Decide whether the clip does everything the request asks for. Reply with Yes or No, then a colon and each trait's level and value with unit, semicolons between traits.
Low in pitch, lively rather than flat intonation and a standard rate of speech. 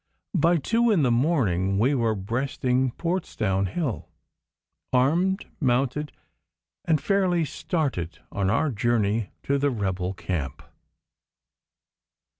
No: low, 130 Hz; wide, 7.7 semitones; slow, 105 wpm